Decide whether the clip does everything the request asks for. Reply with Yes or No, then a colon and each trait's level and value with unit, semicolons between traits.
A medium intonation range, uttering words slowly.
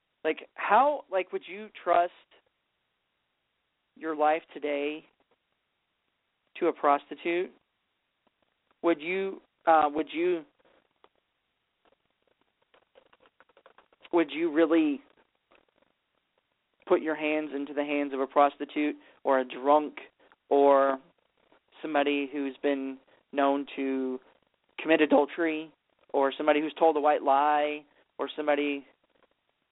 Yes: average, 3.0 semitones; slow, 100 wpm